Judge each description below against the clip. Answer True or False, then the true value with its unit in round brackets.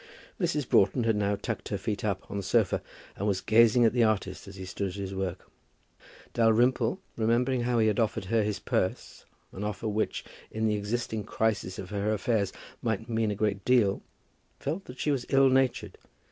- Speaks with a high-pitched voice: False (110 Hz)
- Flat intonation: False (3.0 semitones)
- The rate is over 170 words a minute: True (195 wpm)